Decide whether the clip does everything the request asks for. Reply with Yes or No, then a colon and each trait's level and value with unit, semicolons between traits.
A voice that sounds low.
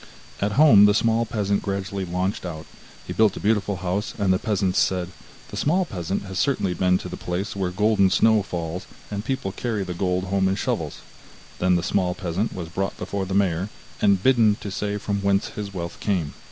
Yes: low, 100 Hz